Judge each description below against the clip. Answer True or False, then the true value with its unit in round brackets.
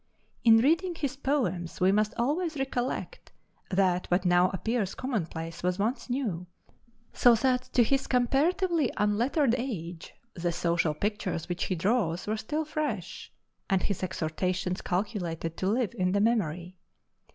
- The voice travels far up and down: True (6.2 semitones)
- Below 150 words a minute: True (140 wpm)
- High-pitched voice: True (205 Hz)